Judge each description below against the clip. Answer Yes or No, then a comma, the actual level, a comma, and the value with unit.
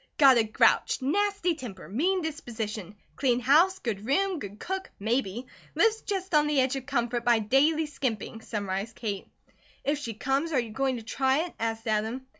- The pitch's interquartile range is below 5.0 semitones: No, wide, 5.4 semitones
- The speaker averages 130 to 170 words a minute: No, average, 180 wpm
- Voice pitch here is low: No, very high, 260 Hz